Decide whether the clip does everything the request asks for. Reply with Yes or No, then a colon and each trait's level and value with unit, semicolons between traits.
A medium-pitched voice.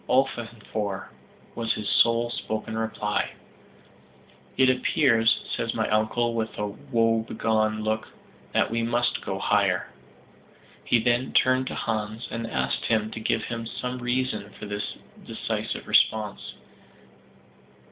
No: low, 115 Hz